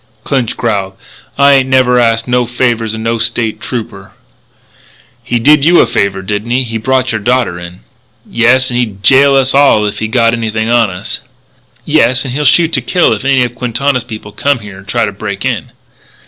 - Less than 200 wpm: No, fast, 205 wpm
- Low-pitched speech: Yes, low, 120 Hz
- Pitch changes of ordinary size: Yes, average, 3.0 semitones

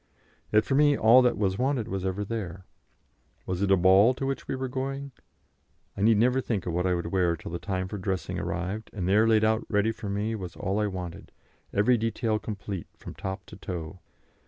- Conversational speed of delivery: No, fast, 215 wpm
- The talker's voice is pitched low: Yes, low, 105 Hz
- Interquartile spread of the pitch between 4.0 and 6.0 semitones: No, average, 3.4 semitones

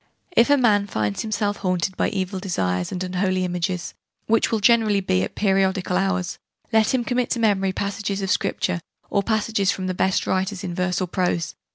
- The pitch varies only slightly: Yes, narrow, 2.2 semitones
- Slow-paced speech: No, average, 190 wpm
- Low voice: No, high, 190 Hz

